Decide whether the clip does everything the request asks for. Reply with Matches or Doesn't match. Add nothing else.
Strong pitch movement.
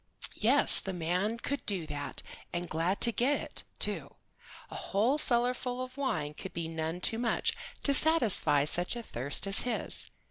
Matches